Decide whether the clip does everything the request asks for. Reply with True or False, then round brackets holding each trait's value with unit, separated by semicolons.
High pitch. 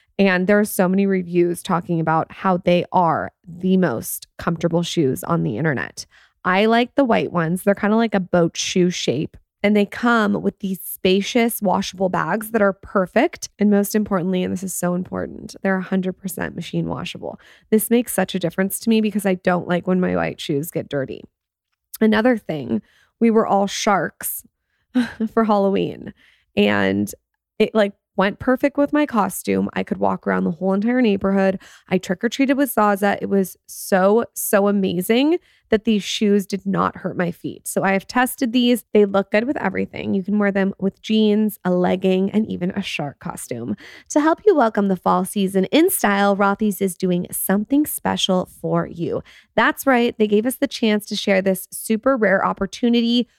True (195 Hz)